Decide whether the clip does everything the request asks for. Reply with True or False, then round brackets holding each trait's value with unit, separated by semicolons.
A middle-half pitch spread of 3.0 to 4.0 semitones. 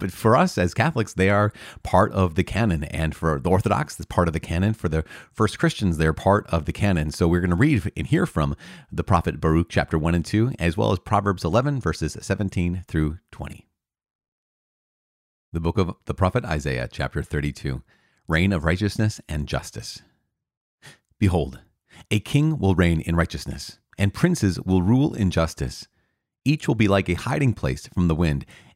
False (4.5 semitones)